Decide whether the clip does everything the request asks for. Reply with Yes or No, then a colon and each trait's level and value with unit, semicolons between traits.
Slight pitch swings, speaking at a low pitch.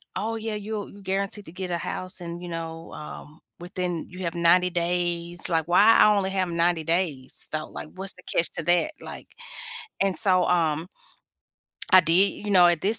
No: narrow, 2.2 semitones; medium, 175 Hz